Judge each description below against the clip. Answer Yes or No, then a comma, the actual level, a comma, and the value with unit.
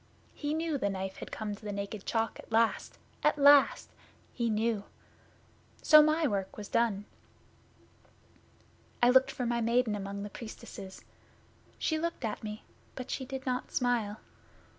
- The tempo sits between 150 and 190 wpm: Yes, average, 155 wpm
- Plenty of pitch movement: No, average, 4.3 semitones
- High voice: Yes, high, 230 Hz